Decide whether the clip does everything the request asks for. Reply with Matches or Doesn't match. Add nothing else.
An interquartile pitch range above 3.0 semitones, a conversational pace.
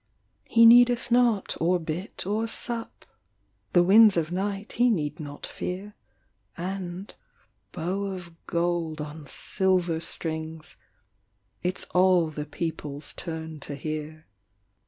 Doesn't match